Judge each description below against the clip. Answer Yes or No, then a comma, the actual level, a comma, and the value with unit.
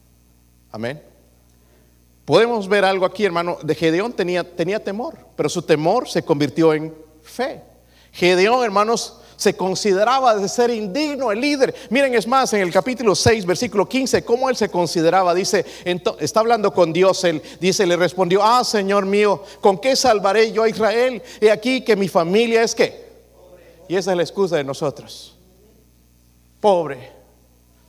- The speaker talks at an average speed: Yes, average, 160 wpm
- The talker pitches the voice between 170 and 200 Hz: Yes, high, 190 Hz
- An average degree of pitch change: No, wide, 6.0 semitones